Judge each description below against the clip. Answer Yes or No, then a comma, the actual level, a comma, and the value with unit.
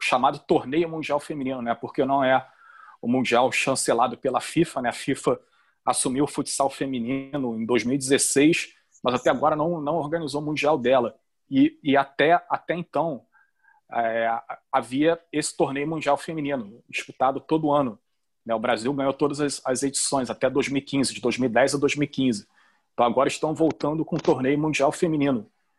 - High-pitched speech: No, medium, 140 Hz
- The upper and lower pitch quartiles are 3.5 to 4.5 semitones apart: No, narrow, 2.6 semitones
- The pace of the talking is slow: No, average, 160 wpm